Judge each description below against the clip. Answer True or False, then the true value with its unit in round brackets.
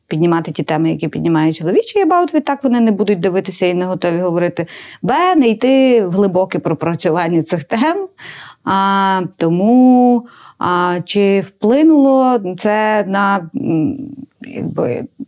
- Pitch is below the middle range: False (195 Hz)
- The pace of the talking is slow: False (125 wpm)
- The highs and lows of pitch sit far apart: True (6.4 semitones)